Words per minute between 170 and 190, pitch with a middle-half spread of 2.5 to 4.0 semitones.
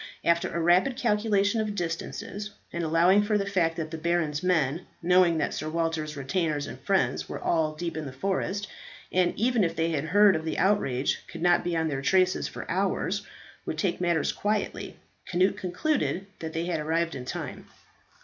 Yes: average, 185 wpm; average, 3.3 semitones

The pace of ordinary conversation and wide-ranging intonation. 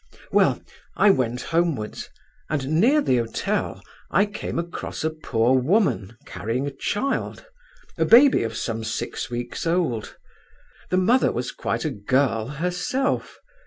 No: slow, 130 wpm; wide, 7.8 semitones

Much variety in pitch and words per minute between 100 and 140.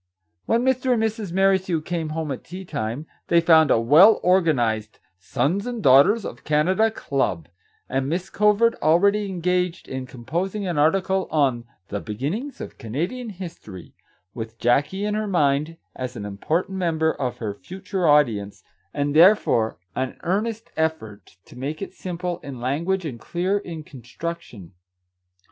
No: wide, 6.7 semitones; average, 160 wpm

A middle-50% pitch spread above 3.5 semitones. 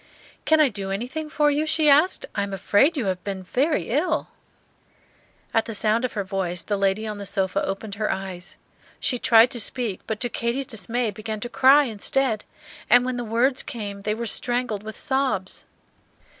Yes: average, 4.4 semitones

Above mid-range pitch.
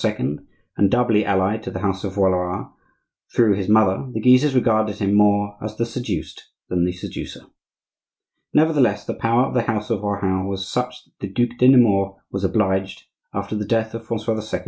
No: low, 105 Hz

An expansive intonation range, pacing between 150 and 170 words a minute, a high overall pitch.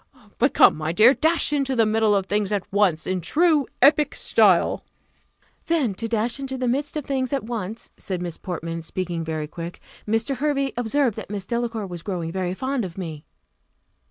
No: wide, 6.7 semitones; average, 190 wpm; high, 220 Hz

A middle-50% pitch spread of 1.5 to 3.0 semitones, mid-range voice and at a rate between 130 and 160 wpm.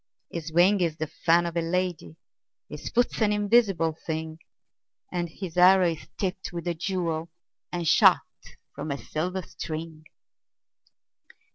Yes: narrow, 2.4 semitones; medium, 170 Hz; average, 140 wpm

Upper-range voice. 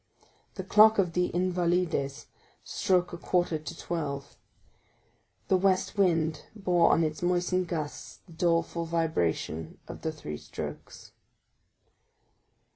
No: medium, 170 Hz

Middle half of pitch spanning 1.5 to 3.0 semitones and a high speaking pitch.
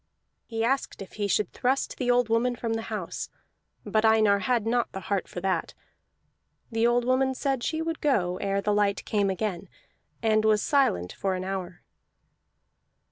No: average, 3.8 semitones; high, 220 Hz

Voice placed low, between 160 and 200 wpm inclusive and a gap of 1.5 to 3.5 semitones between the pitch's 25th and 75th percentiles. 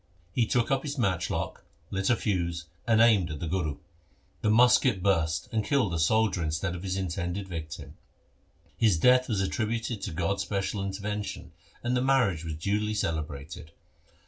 No: very low, 95 Hz; average, 165 wpm; average, 4.8 semitones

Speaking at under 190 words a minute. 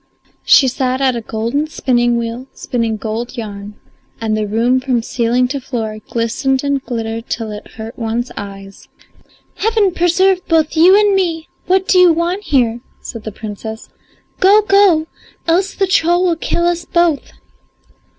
Yes: average, 160 wpm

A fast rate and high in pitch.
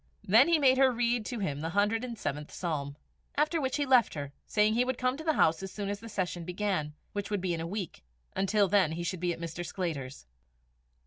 Yes: fast, 240 wpm; high, 200 Hz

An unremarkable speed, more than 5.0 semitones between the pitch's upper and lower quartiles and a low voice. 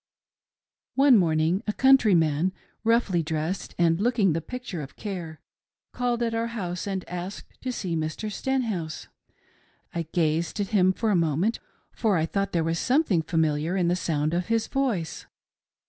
No: average, 160 wpm; wide, 5.5 semitones; medium, 180 Hz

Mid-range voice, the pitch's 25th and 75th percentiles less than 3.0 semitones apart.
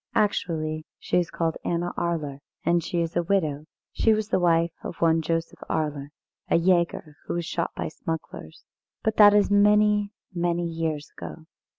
Yes: medium, 170 Hz; narrow, 2.5 semitones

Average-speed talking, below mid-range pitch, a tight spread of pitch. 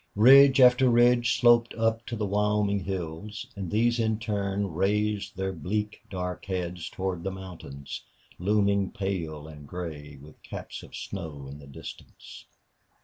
No: average, 145 wpm; low, 100 Hz; average, 3.8 semitones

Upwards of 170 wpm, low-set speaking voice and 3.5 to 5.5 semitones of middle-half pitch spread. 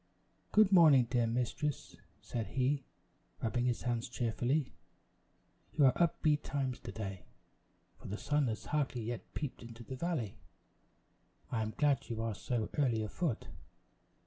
No: average, 145 wpm; low, 125 Hz; average, 4.3 semitones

